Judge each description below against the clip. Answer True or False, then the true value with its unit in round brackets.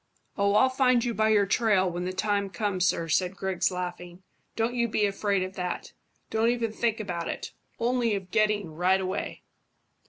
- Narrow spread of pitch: False (3.4 semitones)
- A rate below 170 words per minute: False (185 wpm)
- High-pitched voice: True (200 Hz)